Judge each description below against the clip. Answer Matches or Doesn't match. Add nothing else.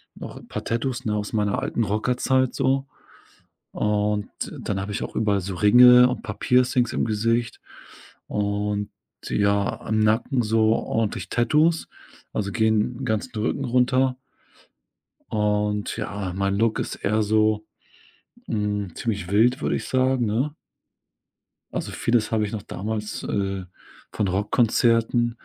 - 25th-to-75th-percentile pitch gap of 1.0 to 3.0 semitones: Matches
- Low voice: Matches